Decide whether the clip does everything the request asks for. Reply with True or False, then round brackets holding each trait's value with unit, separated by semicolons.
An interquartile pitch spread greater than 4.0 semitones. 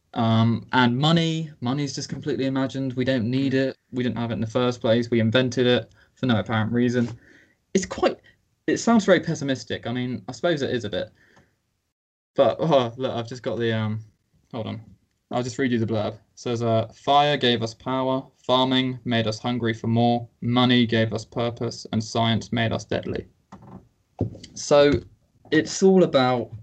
False (2.8 semitones)